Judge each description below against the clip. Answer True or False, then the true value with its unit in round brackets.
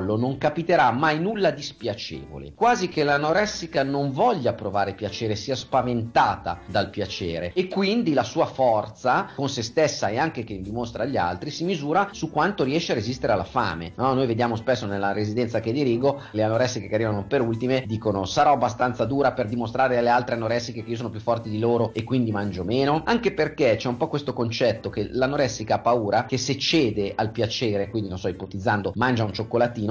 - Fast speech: True (195 wpm)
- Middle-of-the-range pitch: False (120 Hz)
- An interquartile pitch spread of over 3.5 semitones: True (4.6 semitones)